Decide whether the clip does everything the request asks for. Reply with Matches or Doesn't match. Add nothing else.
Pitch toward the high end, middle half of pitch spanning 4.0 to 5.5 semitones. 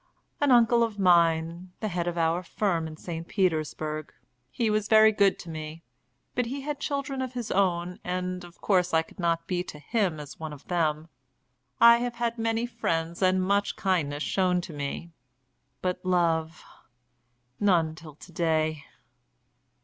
Doesn't match